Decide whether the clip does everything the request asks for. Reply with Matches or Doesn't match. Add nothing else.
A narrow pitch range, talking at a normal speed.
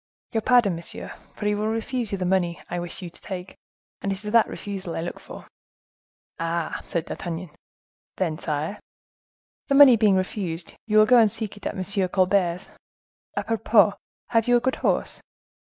Doesn't match